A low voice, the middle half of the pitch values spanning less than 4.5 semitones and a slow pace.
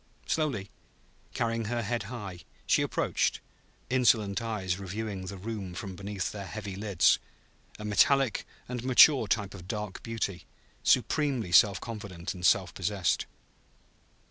Yes: low, 105 Hz; average, 3.2 semitones; slow, 130 wpm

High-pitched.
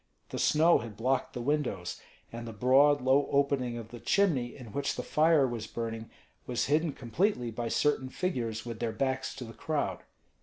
No: low, 130 Hz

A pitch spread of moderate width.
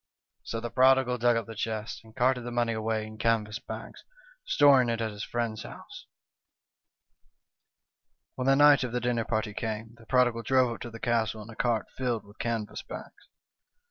No: narrow, 2.0 semitones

